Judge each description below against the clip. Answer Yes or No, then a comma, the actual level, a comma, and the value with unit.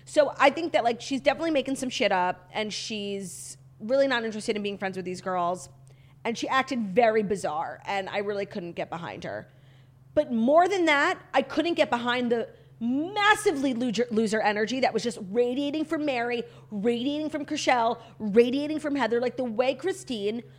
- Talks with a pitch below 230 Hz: No, high, 240 Hz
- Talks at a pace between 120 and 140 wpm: No, average, 185 wpm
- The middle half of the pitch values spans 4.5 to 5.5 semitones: Yes, average, 5.2 semitones